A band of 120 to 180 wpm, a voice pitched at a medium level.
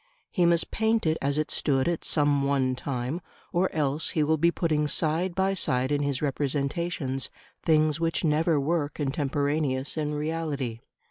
Yes: average, 160 wpm; medium, 150 Hz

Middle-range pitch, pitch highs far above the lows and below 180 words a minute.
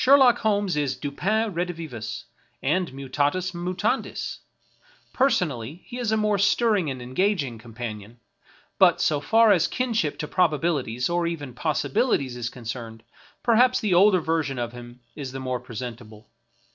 Yes: medium, 155 Hz; wide, 8.2 semitones; average, 140 wpm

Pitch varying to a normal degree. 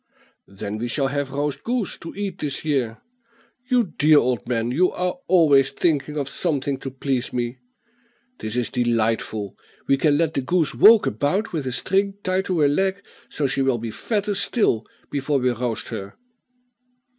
No: wide, 6.4 semitones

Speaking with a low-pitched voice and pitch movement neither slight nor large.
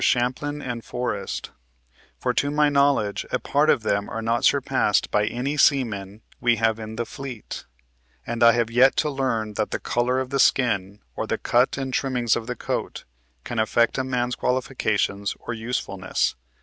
Yes: low, 120 Hz; average, 3.1 semitones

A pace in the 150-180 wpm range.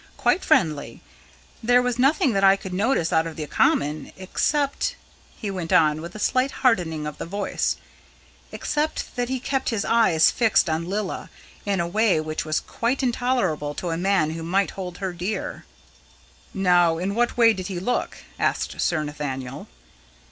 Yes: average, 170 wpm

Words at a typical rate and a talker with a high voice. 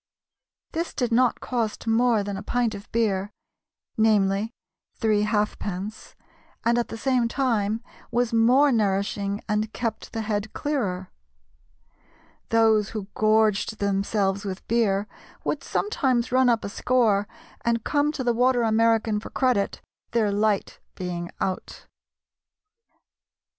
No: slow, 125 wpm; high, 220 Hz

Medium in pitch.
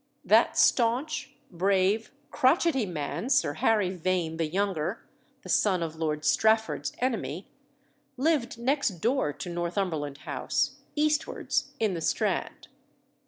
No: high, 195 Hz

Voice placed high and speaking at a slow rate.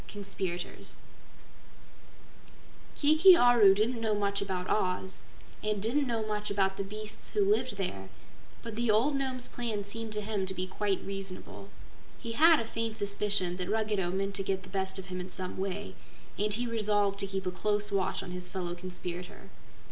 No: high, 200 Hz; average, 180 wpm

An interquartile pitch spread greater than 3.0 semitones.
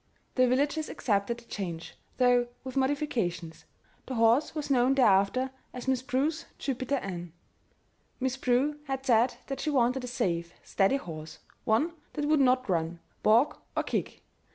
Yes: average, 5.0 semitones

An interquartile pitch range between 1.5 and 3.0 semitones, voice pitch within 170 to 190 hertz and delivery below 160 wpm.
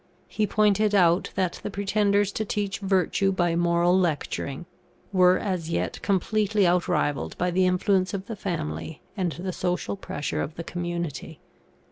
Yes: narrow, 2.5 semitones; medium, 185 Hz; average, 150 wpm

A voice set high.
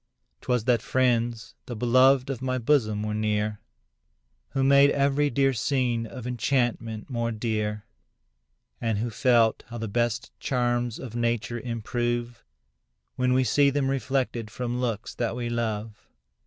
No: low, 120 Hz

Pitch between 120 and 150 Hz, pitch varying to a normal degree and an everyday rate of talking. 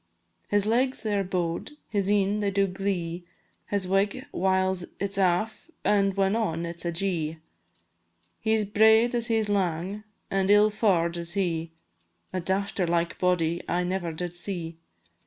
No: high, 190 Hz; average, 3.0 semitones; average, 165 wpm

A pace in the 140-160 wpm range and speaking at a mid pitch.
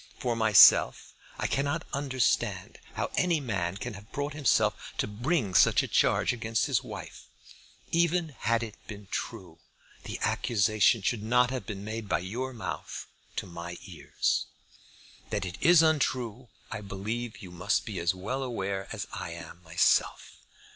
No: average, 155 wpm; low, 110 Hz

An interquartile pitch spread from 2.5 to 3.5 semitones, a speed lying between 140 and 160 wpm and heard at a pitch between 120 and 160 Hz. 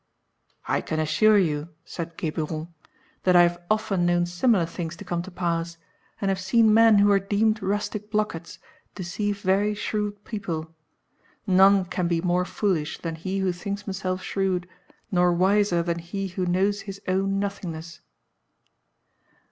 No: average, 2.8 semitones; average, 155 wpm; medium, 185 Hz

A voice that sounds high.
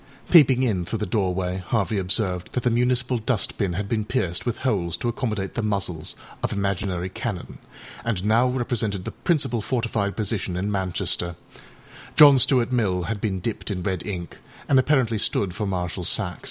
No: low, 105 Hz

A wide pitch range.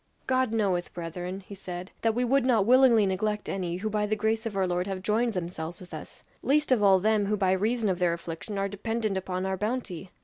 No: average, 3.4 semitones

